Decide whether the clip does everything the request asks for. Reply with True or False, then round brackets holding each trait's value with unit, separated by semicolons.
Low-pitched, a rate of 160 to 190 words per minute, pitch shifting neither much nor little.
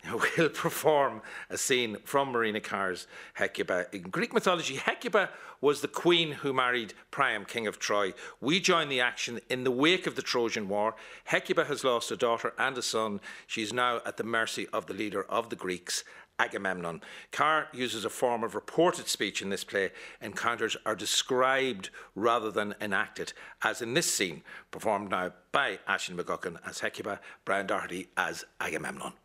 True (125 Hz; 170 wpm; 4.1 semitones)